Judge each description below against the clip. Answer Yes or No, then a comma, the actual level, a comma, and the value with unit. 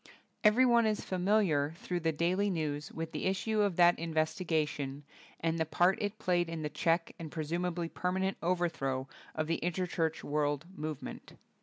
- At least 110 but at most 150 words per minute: No, average, 160 wpm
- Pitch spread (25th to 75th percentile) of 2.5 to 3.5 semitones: Yes, average, 2.8 semitones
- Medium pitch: Yes, medium, 170 Hz